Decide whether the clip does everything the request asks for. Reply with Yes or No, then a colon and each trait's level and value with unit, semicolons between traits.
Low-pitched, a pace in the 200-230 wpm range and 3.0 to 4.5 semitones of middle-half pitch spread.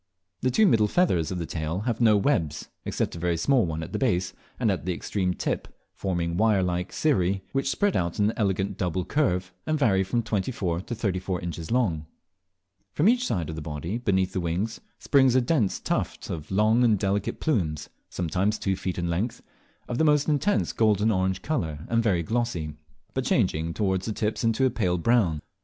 No: very low, 95 Hz; fast, 205 wpm; average, 5.1 semitones